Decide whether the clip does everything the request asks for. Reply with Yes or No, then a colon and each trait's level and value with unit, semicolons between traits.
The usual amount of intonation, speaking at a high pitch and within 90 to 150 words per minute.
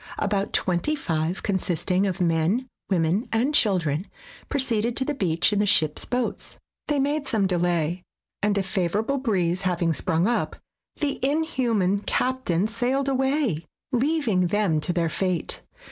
No: wide, 6.5 semitones; high, 200 Hz; average, 145 wpm